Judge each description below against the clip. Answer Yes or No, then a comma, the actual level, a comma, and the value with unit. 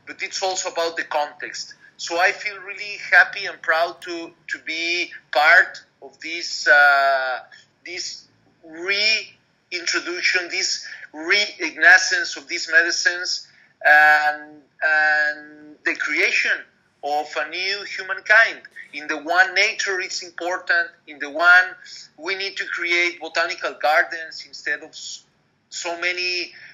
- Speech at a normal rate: No, slow, 120 wpm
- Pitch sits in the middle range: Yes, medium, 175 Hz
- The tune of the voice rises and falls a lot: No, average, 4.5 semitones